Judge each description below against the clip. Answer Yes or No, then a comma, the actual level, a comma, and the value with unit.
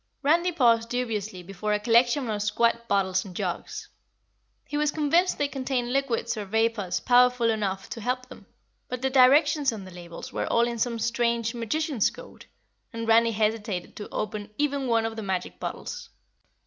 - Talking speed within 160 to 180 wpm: Yes, average, 175 wpm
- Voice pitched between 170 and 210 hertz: No, high, 230 Hz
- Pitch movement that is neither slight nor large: Yes, average, 3.3 semitones